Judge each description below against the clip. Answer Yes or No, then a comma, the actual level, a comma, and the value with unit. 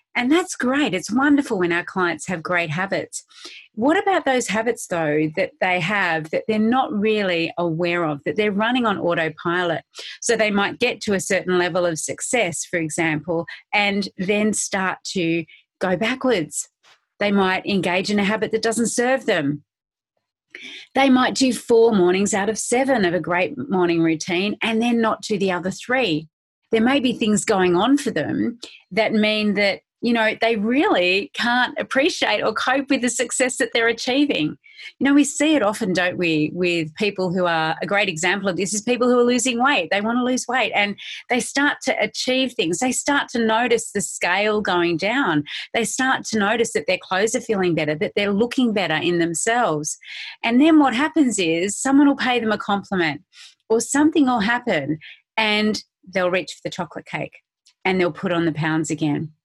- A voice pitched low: No, high, 210 Hz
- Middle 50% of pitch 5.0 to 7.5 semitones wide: Yes, wide, 5.5 semitones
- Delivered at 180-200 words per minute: Yes, average, 190 wpm